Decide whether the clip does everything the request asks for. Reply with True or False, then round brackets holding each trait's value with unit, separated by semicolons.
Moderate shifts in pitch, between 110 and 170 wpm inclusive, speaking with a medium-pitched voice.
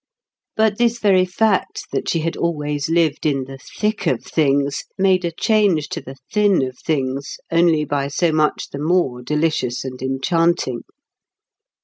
True (4.8 semitones; 155 wpm; 160 Hz)